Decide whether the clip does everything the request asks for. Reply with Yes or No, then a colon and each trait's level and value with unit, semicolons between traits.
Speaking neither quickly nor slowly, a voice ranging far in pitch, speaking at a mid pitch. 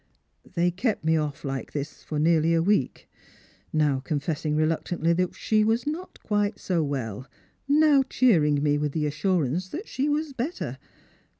Yes: average, 165 wpm; wide, 6.4 semitones; medium, 165 Hz